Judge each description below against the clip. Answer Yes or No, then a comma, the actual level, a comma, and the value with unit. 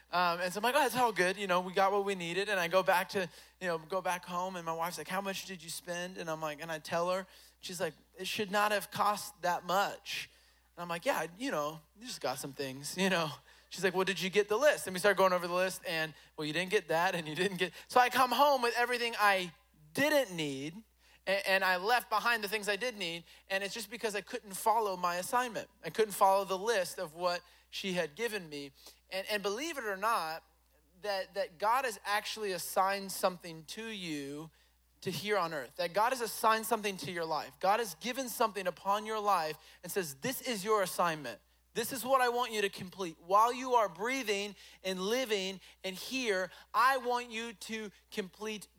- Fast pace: Yes, fast, 230 wpm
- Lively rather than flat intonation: No, average, 3.8 semitones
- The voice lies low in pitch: No, high, 195 Hz